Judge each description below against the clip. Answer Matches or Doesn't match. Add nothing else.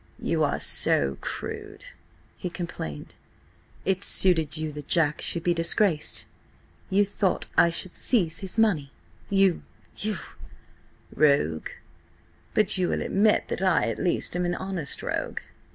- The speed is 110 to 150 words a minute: Matches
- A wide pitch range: Doesn't match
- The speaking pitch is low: Doesn't match